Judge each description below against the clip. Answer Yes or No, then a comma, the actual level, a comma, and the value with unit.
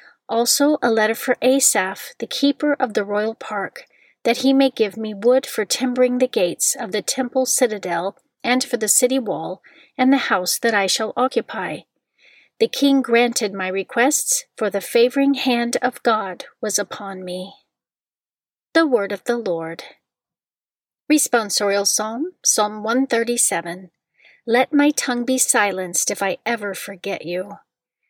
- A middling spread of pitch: Yes, average, 4.4 semitones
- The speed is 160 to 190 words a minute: No, average, 150 wpm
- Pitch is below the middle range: No, high, 235 Hz